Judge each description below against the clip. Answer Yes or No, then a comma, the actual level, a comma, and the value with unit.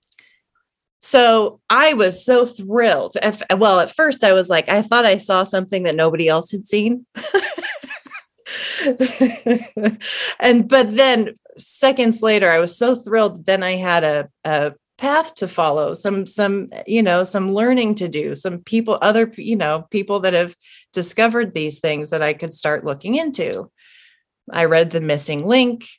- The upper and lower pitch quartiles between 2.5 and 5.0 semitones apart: No, wide, 5.6 semitones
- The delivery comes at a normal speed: Yes, average, 155 wpm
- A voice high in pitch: Yes, high, 210 Hz